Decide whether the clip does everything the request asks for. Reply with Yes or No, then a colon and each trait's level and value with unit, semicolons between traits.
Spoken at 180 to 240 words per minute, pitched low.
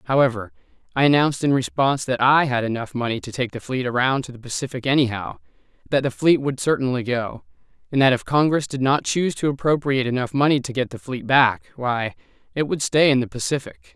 Yes: fast, 205 wpm; low, 130 Hz